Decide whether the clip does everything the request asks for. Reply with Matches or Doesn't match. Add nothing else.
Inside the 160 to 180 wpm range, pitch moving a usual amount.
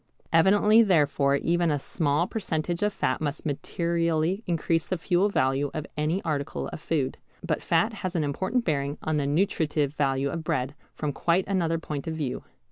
Matches